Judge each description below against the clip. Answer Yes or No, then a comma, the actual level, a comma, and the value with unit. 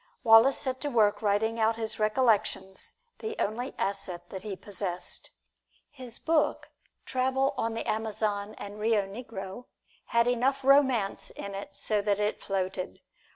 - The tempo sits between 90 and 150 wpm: Yes, average, 145 wpm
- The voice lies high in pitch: Yes, high, 220 Hz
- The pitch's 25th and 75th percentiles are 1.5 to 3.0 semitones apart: No, average, 3.6 semitones